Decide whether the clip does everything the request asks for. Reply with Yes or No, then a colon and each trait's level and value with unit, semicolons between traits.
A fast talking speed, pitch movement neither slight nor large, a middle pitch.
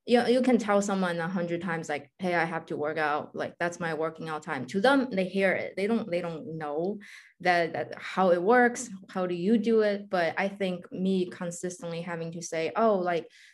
Yes: fast, 230 wpm; average, 3.5 semitones; medium, 180 Hz